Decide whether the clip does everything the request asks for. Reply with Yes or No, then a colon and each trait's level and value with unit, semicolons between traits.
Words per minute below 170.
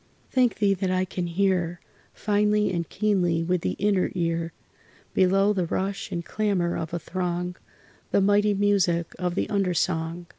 Yes: average, 160 wpm